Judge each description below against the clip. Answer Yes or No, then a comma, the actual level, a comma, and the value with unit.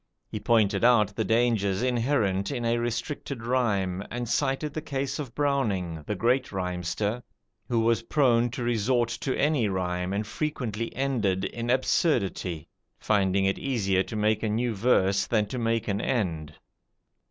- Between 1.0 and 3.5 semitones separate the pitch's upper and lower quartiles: No, average, 3.9 semitones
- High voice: No, low, 115 Hz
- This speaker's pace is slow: No, average, 155 wpm